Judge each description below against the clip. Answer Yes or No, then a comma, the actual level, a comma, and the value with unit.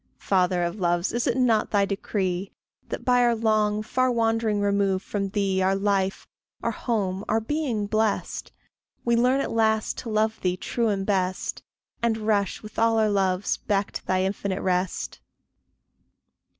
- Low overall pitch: No, high, 205 Hz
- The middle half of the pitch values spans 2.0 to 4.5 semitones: Yes, average, 2.7 semitones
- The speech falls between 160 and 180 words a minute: Yes, average, 165 wpm